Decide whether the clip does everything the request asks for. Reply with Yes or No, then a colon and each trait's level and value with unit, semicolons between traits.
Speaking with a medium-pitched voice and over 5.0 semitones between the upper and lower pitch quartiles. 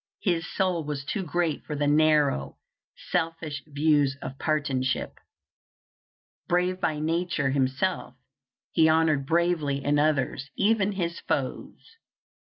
No: medium, 155 Hz; average, 3.3 semitones